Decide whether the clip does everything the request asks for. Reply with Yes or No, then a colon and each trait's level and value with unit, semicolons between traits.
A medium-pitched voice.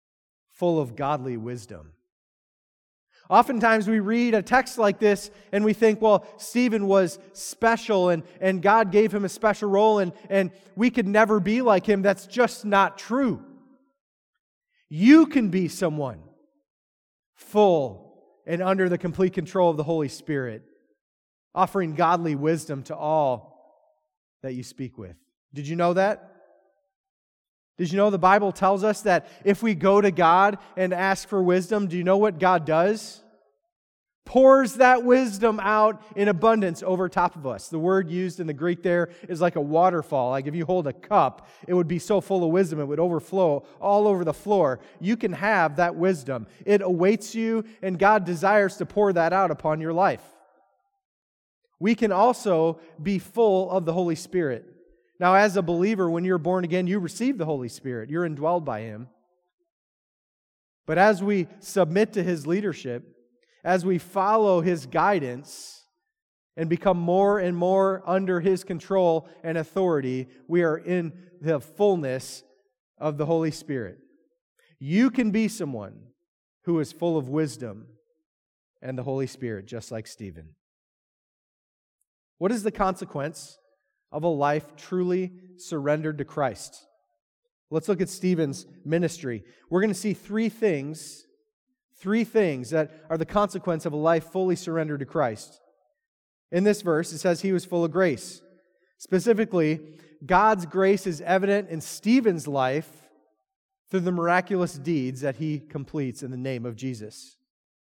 Yes: medium, 180 Hz